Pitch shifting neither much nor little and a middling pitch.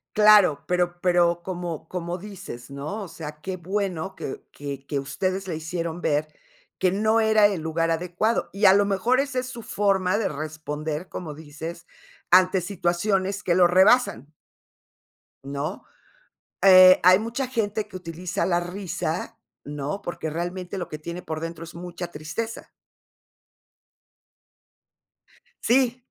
Yes: average, 3.6 semitones; medium, 180 Hz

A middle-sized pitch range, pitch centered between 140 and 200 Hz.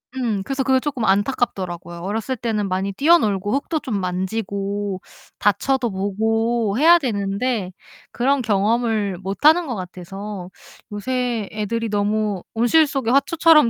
No: average, 4.5 semitones; high, 215 Hz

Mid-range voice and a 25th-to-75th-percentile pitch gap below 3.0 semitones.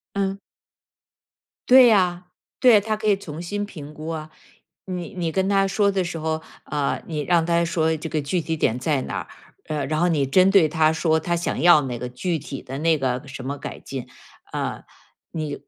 No: medium, 160 Hz; average, 3.7 semitones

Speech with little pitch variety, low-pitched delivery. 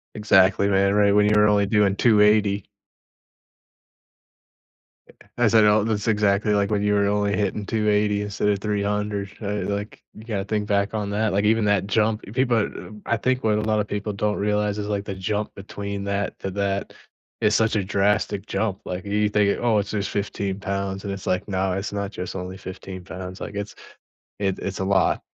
Yes: narrow, 1.1 semitones; low, 105 Hz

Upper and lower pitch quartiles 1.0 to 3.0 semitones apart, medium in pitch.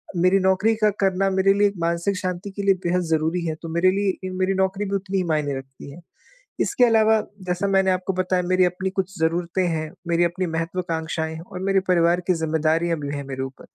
Yes: average, 2.7 semitones; medium, 180 Hz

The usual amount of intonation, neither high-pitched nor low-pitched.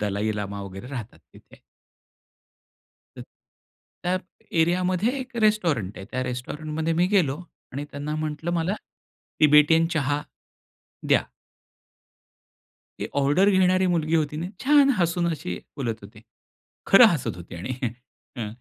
No: wide, 6.3 semitones; medium, 155 Hz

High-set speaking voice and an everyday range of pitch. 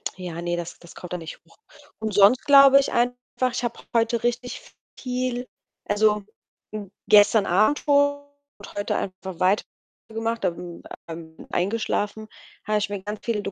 Yes: high, 210 Hz; average, 4.5 semitones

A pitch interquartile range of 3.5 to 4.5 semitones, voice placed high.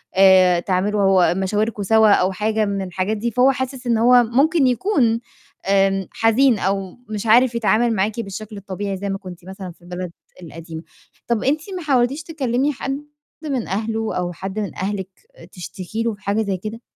Yes: average, 3.9 semitones; high, 210 Hz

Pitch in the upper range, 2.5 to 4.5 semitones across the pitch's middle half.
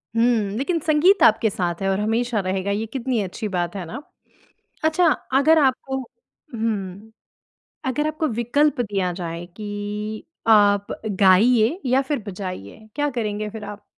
No: high, 220 Hz; average, 5.1 semitones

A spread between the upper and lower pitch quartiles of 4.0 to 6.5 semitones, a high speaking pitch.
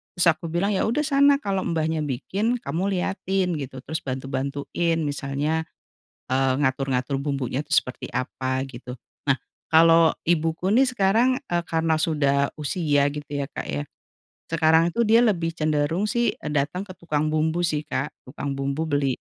No: average, 4.3 semitones; medium, 160 Hz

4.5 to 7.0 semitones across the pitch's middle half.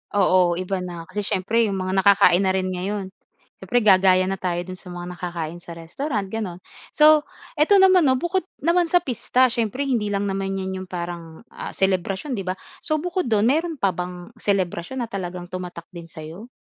Yes: average, 5.0 semitones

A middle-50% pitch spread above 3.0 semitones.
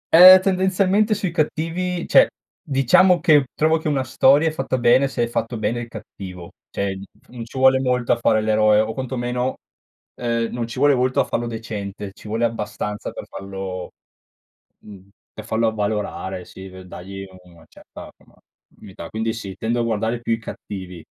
Yes: average, 4.5 semitones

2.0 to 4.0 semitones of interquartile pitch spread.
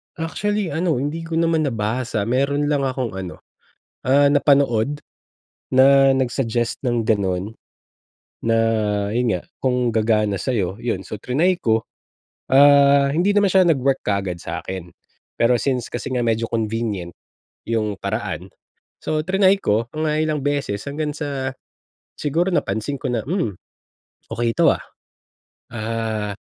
No: average, 4.7 semitones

